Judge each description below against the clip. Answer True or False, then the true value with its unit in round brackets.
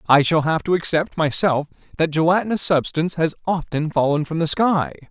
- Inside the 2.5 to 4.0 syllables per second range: False (5.5 syllables/s)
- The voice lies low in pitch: False (160 Hz)